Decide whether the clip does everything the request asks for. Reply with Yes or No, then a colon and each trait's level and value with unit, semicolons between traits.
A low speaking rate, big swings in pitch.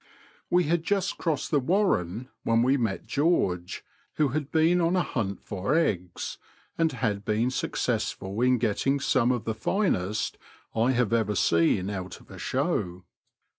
No: average, 160 wpm; wide, 7.5 semitones